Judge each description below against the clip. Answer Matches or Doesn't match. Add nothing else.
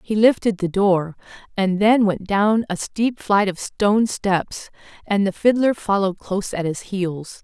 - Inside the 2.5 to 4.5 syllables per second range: Matches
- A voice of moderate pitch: Doesn't match